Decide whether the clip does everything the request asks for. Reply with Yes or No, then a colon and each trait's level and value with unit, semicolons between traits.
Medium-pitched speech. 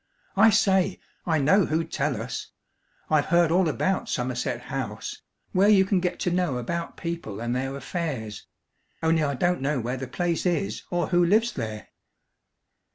Yes: medium, 160 Hz